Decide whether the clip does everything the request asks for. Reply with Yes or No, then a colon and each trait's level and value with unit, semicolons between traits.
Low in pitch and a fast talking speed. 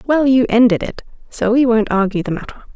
No: high, 230 Hz; fast, 220 wpm